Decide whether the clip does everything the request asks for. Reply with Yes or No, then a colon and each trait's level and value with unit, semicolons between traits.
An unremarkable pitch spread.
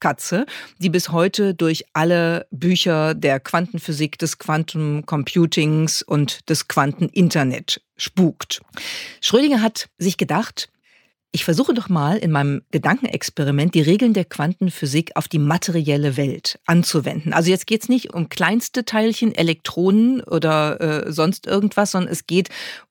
Yes: average, 3.5 semitones